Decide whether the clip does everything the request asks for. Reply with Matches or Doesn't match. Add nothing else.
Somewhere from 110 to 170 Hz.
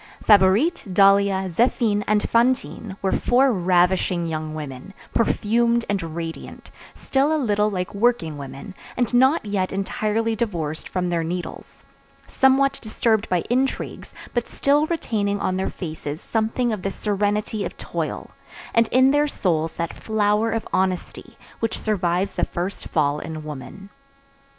Doesn't match